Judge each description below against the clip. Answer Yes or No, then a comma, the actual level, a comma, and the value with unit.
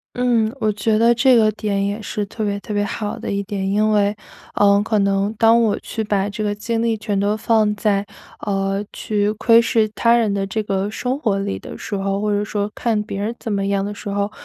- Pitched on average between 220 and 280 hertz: No, high, 210 Hz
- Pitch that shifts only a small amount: Yes, narrow, 1.6 semitones